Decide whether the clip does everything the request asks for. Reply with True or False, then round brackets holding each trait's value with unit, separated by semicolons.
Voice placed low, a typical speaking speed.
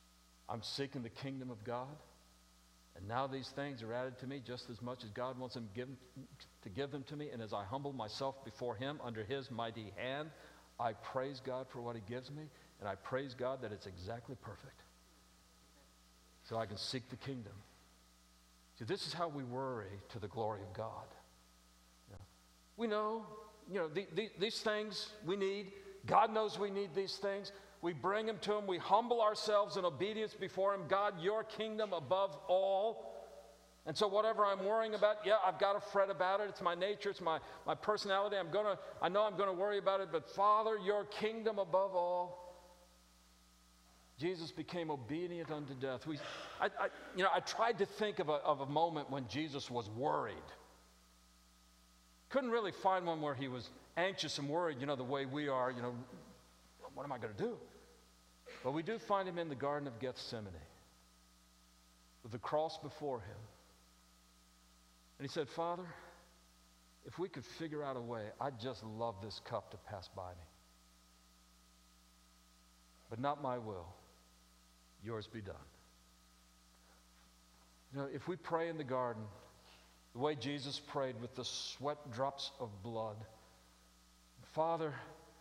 True (130 Hz; 175 wpm)